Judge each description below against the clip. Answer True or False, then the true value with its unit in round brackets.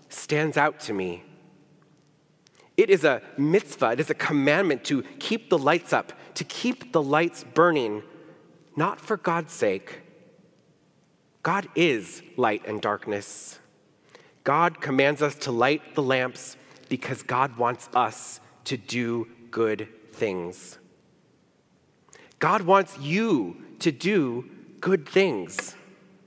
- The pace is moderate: False (120 wpm)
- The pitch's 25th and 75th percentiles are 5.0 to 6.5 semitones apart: True (5.6 semitones)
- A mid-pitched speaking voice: True (150 Hz)